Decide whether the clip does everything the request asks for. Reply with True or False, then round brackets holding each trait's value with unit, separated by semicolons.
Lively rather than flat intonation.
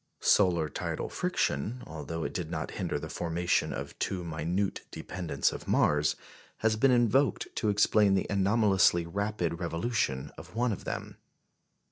False (4.4 semitones)